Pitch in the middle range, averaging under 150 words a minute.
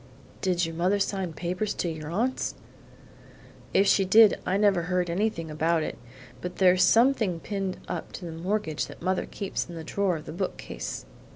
No: medium, 180 Hz; average, 180 wpm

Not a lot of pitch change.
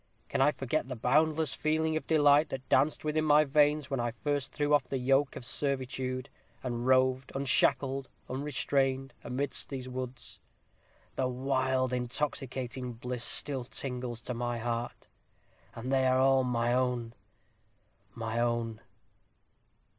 Yes: narrow, 2.2 semitones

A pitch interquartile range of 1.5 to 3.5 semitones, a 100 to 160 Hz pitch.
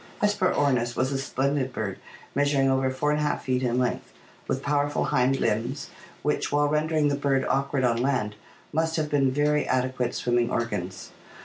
Yes: narrow, 2.6 semitones; low, 135 Hz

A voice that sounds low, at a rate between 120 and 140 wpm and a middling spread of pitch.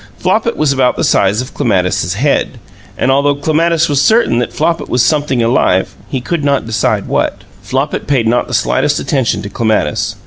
No: low, 130 Hz; average, 180 wpm; average, 4.7 semitones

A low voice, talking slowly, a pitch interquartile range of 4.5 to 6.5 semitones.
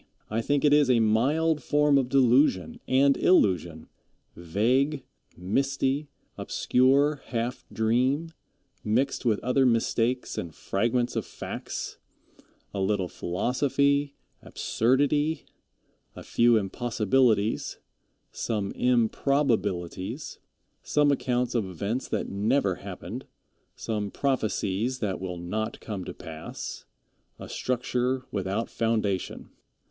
Yes: low, 120 Hz; slow, 105 wpm; average, 4.9 semitones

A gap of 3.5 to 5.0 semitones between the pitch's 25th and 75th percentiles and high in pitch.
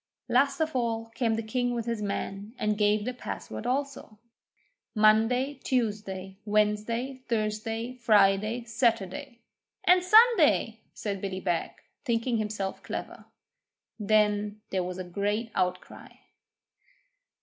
No: average, 2.9 semitones; high, 220 Hz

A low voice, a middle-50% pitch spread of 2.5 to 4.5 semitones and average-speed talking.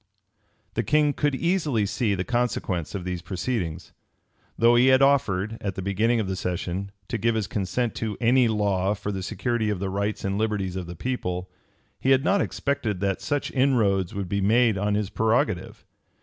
Yes: low, 105 Hz; average, 4.0 semitones; average, 190 wpm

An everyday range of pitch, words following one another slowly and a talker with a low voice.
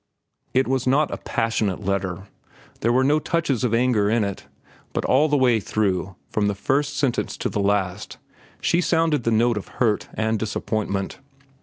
No: average, 4.5 semitones; average, 175 wpm; low, 115 Hz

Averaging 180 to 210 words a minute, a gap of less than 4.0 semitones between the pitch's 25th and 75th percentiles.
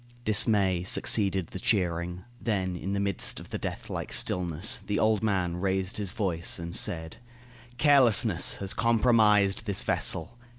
No: average, 145 wpm; average, 3.3 semitones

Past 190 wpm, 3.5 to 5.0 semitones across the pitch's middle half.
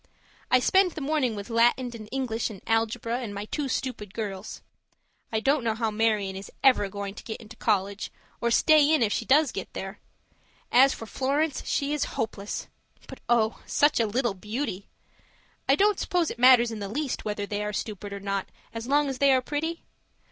Yes: average, 200 wpm; average, 4.5 semitones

